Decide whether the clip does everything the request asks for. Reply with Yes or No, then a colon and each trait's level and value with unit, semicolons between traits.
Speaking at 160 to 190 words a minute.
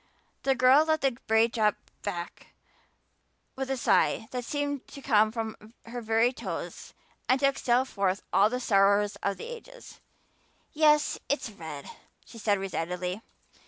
No: average, 150 wpm